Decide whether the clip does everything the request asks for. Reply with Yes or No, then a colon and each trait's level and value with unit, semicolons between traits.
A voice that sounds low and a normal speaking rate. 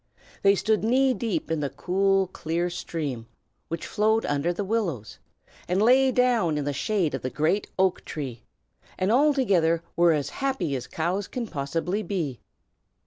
No: medium, 180 Hz; average, 160 wpm